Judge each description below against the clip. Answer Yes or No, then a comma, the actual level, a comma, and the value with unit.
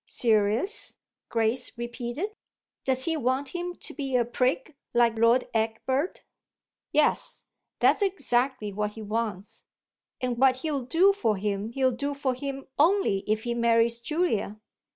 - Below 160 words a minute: Yes, average, 140 wpm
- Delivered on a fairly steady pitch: No, average, 3.9 semitones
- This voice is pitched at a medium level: No, very high, 250 Hz